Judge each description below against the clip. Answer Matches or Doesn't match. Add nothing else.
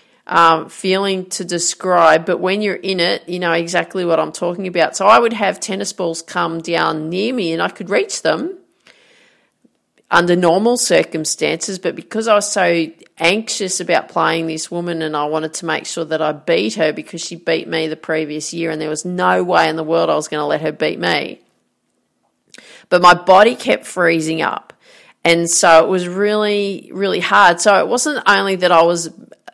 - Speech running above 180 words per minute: Matches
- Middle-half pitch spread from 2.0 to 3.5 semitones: Matches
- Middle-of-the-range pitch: Matches